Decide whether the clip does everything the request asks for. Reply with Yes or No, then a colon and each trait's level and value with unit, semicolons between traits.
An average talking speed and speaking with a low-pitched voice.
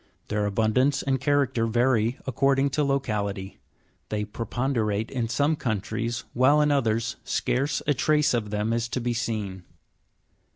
Yes: average, 150 wpm; low, 120 Hz